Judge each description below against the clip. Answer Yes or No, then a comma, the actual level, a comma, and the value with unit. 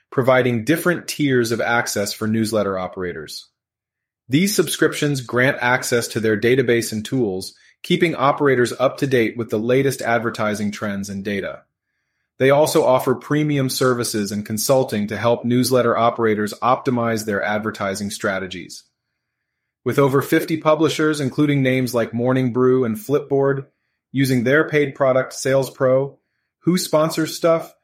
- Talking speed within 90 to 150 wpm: Yes, slow, 135 wpm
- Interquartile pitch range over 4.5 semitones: No, average, 4.2 semitones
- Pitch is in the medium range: No, low, 125 Hz